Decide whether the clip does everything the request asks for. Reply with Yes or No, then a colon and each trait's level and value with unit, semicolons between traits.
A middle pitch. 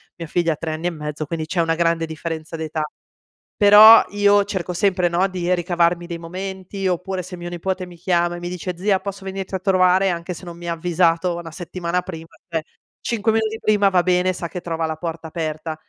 Yes: medium, 175 Hz